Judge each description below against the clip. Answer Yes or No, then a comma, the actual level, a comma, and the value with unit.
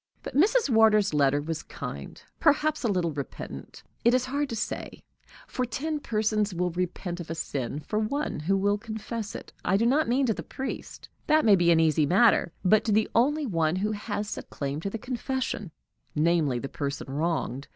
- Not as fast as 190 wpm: No, average, 195 wpm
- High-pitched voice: Yes, high, 205 Hz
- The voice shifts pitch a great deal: Yes, wide, 6.6 semitones